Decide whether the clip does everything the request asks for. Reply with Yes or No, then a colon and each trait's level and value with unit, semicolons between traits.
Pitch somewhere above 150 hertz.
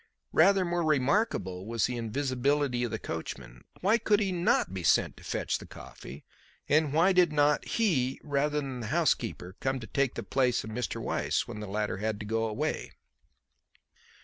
No: low, 135 Hz